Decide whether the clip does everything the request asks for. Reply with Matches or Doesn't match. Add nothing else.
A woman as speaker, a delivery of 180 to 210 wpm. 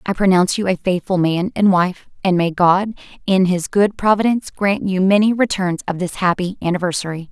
Matches